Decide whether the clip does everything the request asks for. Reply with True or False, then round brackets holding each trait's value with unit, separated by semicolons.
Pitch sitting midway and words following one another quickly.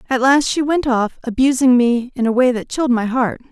False (250 Hz; 240 wpm)